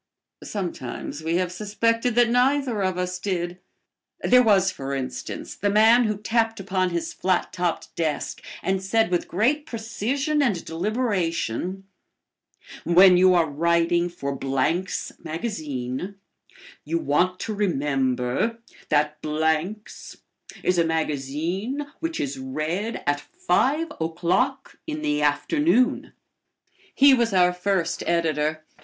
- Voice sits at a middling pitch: Yes, medium, 180 Hz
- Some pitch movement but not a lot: No, wide, 5.9 semitones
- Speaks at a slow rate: Yes, slow, 125 wpm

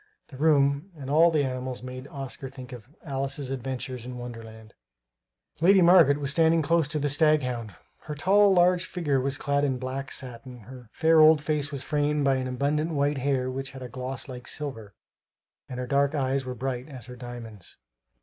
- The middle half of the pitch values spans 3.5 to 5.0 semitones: No, average, 2.8 semitones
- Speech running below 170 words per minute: No, average, 185 wpm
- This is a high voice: No, low, 135 Hz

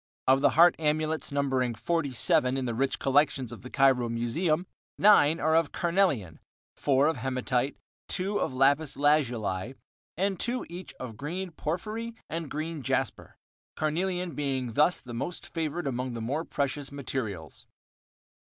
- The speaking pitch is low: No, medium, 145 Hz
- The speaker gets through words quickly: No, average, 145 wpm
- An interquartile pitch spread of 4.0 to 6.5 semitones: Yes, average, 4.5 semitones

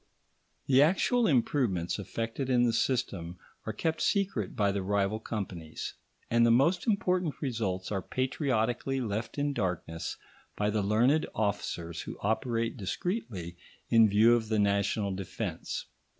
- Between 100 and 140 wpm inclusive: Yes, slow, 135 wpm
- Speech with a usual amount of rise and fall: Yes, average, 4.9 semitones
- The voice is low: Yes, low, 115 Hz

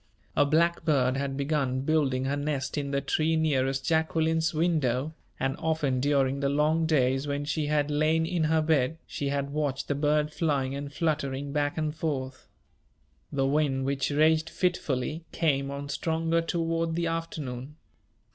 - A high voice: No, medium, 145 Hz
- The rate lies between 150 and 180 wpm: Yes, average, 155 wpm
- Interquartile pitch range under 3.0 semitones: Yes, narrow, 2.6 semitones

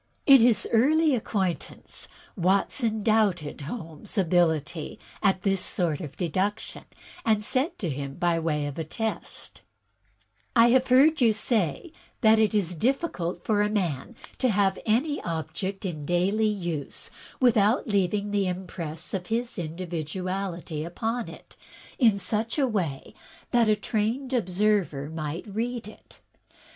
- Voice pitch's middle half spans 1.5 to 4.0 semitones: No, average, 4.6 semitones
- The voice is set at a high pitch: Yes, high, 200 Hz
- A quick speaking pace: No, slow, 135 wpm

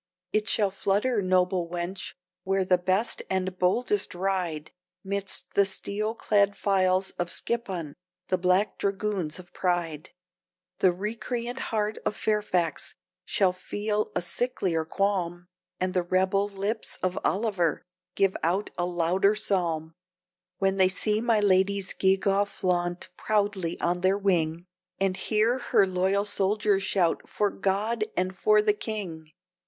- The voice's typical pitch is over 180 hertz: Yes, high, 190 Hz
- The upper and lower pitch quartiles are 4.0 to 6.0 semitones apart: No, narrow, 2.4 semitones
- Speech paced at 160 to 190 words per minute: No, slow, 135 wpm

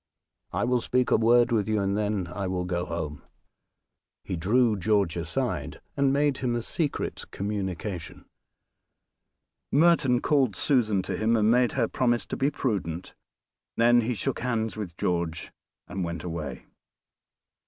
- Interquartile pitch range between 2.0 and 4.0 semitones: No, wide, 5.4 semitones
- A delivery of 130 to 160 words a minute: Yes, average, 150 wpm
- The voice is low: Yes, low, 110 Hz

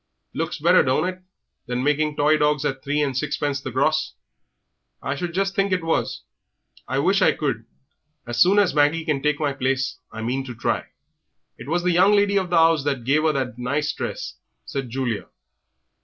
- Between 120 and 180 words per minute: No, average, 195 wpm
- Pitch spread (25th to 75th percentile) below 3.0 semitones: No, average, 3.9 semitones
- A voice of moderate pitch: Yes, medium, 150 Hz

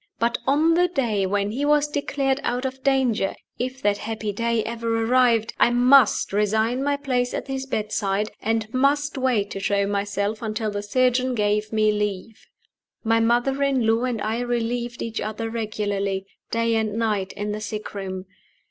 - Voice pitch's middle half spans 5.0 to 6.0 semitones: No, average, 3.3 semitones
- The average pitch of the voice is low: No, high, 225 Hz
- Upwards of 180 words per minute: No, average, 175 wpm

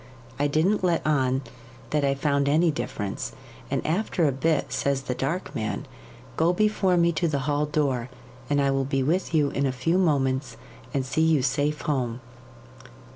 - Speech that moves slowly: No, average, 180 wpm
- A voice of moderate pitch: Yes, medium, 145 Hz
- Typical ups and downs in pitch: Yes, average, 3.2 semitones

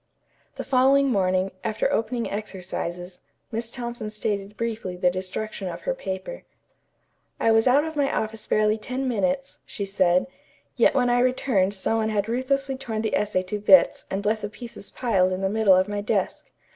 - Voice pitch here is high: Yes, high, 215 Hz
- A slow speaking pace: No, average, 180 wpm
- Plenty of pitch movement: No, average, 4.2 semitones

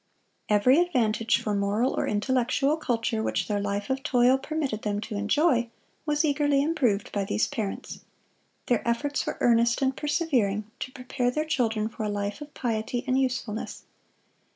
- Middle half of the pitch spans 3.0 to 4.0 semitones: No, average, 4.5 semitones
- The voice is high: Yes, high, 245 Hz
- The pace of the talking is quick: No, average, 160 wpm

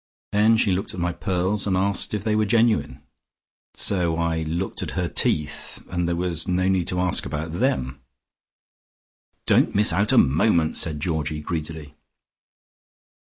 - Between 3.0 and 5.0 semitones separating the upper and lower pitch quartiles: Yes, average, 3.7 semitones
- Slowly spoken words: No, average, 160 wpm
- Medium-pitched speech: No, very low, 90 Hz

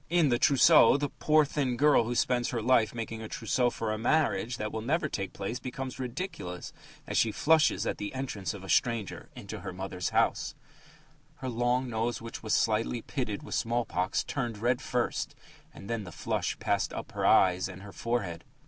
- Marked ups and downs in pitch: No, average, 3.4 semitones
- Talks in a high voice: No, low, 115 Hz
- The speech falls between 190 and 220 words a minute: Yes, average, 200 wpm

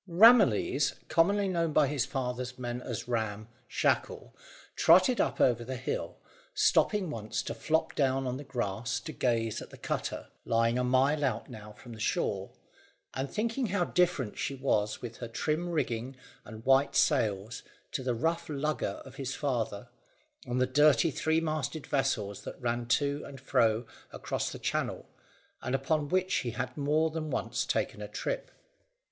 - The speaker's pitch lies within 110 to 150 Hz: Yes, low, 135 Hz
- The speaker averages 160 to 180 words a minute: Yes, average, 165 wpm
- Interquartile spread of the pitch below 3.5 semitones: No, average, 4.6 semitones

